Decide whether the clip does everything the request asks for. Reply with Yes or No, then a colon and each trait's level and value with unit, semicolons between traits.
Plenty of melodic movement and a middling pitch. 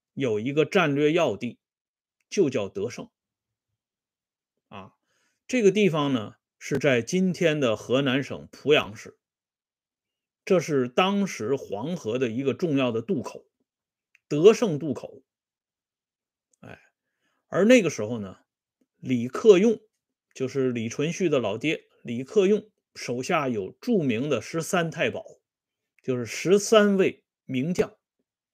Yes: wide, 7.9 semitones; medium, 150 Hz